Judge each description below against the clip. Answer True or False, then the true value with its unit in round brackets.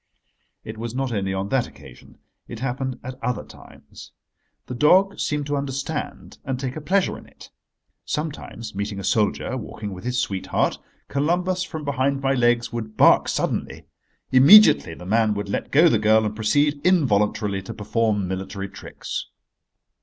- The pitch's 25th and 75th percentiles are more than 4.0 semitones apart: True (5.2 semitones)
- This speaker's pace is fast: False (160 wpm)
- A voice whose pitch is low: True (125 Hz)